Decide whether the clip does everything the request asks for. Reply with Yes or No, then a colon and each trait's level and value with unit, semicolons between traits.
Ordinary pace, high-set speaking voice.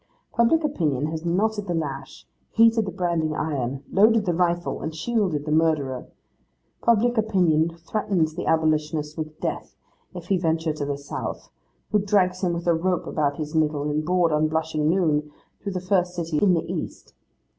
No: average, 170 wpm; medium, 165 Hz